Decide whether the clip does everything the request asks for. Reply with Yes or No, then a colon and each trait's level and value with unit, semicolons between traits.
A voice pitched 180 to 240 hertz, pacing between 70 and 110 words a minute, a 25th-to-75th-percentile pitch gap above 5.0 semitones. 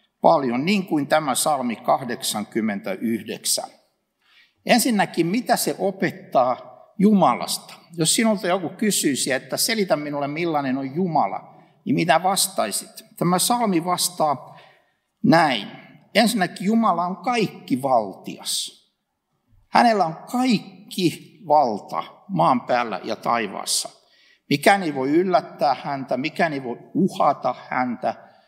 Yes: high, 190 Hz; average, 105 wpm; wide, 5.5 semitones